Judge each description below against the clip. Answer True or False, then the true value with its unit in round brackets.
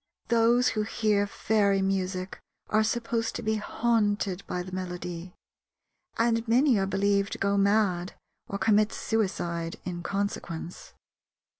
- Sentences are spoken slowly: True (130 wpm)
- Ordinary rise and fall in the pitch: True (3.0 semitones)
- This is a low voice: False (200 Hz)